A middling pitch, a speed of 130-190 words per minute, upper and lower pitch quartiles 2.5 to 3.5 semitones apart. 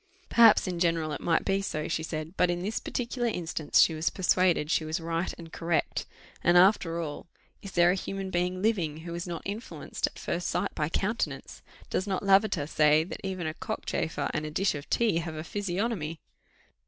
No: medium, 175 Hz; average, 200 wpm; average, 3.2 semitones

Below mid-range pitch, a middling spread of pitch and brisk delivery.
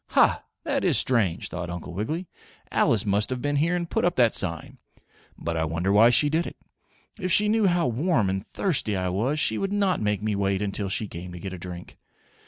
No: low, 105 Hz; wide, 8.9 semitones; fast, 220 wpm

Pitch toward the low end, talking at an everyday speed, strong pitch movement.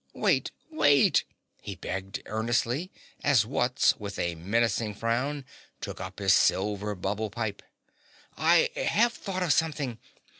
No: low, 115 Hz; slow, 125 wpm; wide, 5.7 semitones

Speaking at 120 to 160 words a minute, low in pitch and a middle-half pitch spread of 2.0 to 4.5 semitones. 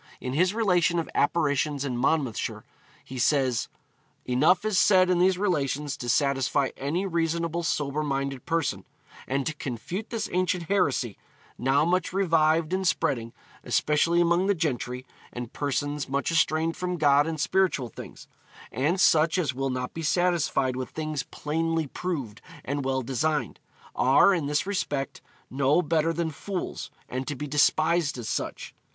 No: average, 155 wpm; medium, 155 Hz; average, 4.0 semitones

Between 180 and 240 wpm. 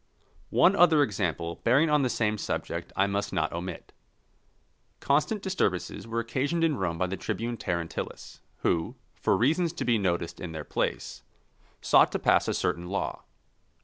No: average, 160 wpm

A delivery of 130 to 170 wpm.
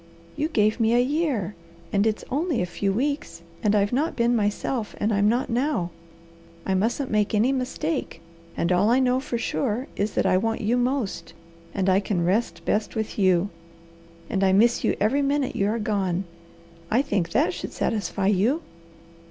No: average, 185 wpm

